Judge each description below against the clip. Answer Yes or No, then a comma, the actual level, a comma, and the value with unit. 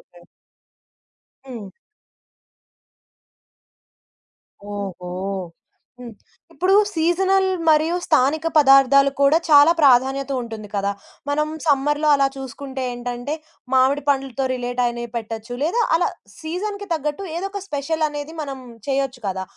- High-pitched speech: Yes, very high, 275 Hz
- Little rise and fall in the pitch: No, average, 4.2 semitones